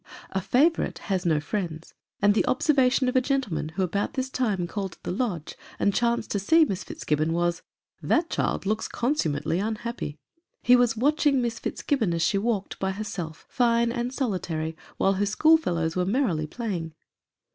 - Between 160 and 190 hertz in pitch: No, high, 205 Hz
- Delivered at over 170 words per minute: Yes, average, 180 wpm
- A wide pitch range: Yes, wide, 6.4 semitones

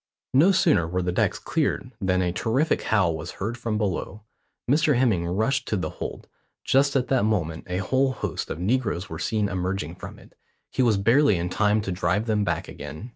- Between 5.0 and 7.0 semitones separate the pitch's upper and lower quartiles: Yes, wide, 5.5 semitones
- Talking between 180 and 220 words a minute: Yes, average, 200 wpm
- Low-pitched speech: Yes, low, 105 Hz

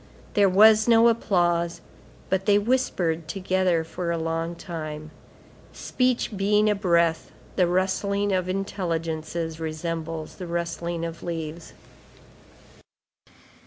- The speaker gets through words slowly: Yes, slow, 110 wpm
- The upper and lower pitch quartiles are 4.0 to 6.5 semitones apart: No, average, 3.3 semitones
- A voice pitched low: No, medium, 175 Hz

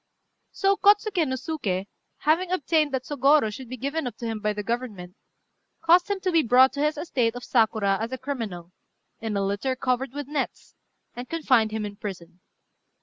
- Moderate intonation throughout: No, wide, 5.8 semitones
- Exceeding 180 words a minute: Yes, average, 190 wpm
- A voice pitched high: Yes, very high, 255 Hz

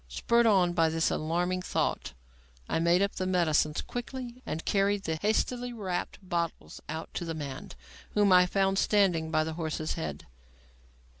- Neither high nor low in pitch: Yes, medium, 180 Hz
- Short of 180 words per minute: Yes, average, 160 wpm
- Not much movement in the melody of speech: No, average, 3.9 semitones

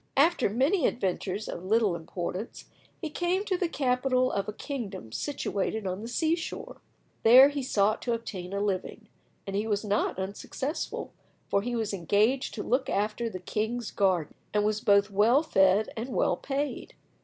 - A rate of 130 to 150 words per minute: No, average, 170 wpm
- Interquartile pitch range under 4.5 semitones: No, average, 4.8 semitones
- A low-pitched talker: No, high, 215 Hz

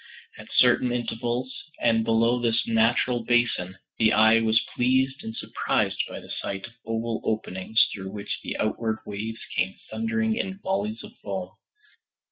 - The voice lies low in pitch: Yes, low, 115 Hz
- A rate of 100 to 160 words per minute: Yes, average, 150 wpm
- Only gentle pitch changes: Yes, narrow, 2.0 semitones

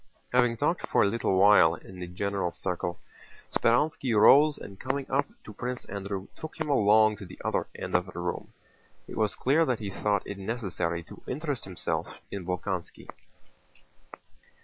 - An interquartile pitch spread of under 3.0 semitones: No, average, 5.2 semitones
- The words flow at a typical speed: Yes, average, 170 wpm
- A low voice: Yes, low, 105 Hz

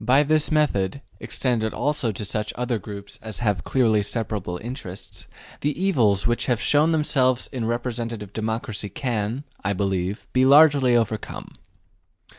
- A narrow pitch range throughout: No, average, 4.2 semitones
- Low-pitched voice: Yes, low, 115 Hz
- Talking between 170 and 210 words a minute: No, average, 140 wpm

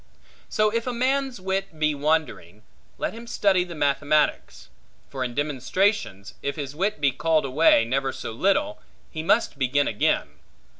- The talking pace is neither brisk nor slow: Yes, average, 155 wpm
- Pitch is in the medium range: Yes, medium, 155 Hz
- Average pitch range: No, wide, 6.4 semitones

